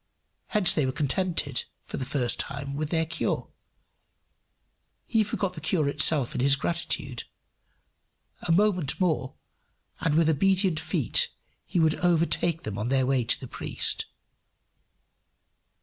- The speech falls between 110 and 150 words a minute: Yes, slow, 135 wpm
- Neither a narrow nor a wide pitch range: Yes, average, 4.3 semitones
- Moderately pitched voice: Yes, medium, 155 Hz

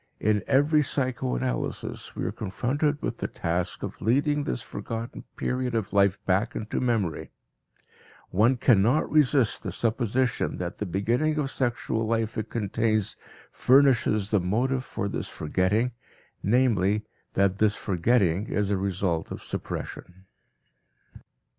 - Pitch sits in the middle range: No, low, 110 Hz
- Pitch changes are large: No, average, 4.5 semitones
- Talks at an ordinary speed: No, slow, 130 wpm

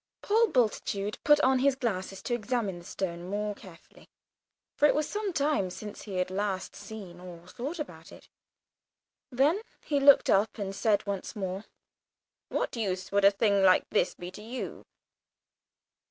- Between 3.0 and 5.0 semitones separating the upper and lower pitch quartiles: No, wide, 5.4 semitones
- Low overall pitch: No, high, 205 Hz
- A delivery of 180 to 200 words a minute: No, average, 165 wpm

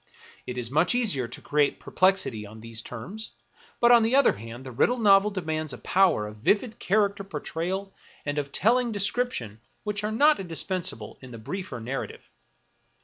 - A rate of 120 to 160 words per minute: No, average, 175 wpm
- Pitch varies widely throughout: Yes, wide, 9.0 semitones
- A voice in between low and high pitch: Yes, medium, 180 Hz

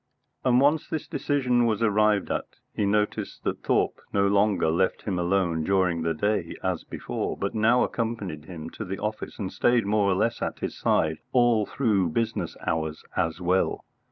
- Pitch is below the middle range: Yes, low, 100 Hz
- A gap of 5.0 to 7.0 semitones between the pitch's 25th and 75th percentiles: No, average, 4.3 semitones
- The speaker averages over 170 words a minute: Yes, average, 180 wpm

